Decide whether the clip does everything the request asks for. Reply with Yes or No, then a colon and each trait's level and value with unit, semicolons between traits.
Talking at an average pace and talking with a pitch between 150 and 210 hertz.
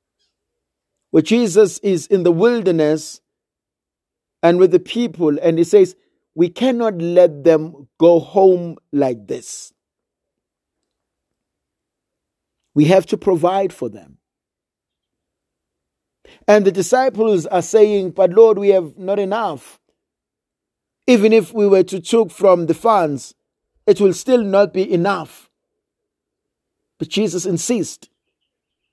No: slow, 115 wpm; high, 190 Hz